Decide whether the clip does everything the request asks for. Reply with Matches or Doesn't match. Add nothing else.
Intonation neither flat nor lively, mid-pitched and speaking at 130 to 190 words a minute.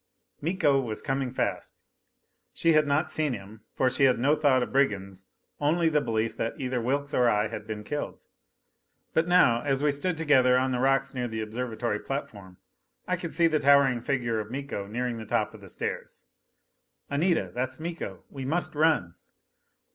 Doesn't match